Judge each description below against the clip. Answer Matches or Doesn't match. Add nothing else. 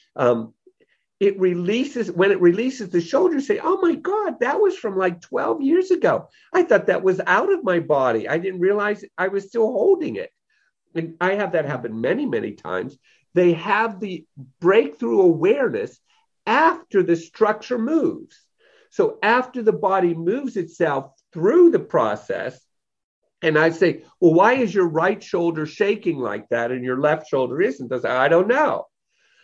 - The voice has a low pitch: Doesn't match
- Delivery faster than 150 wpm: Matches